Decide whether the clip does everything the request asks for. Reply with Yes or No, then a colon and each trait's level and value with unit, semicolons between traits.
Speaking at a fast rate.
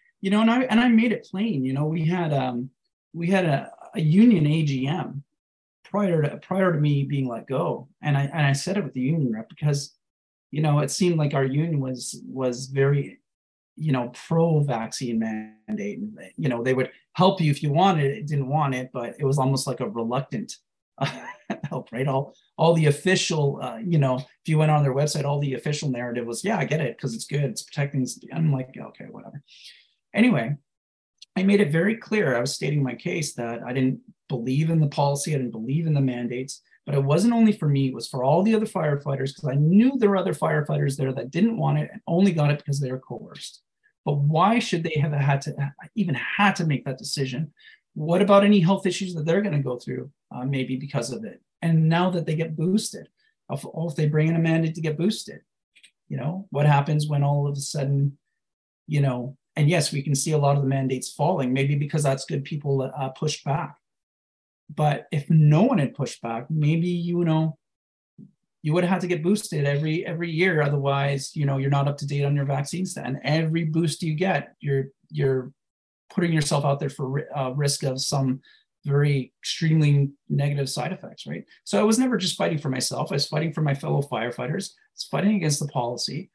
Yes: fast, 220 wpm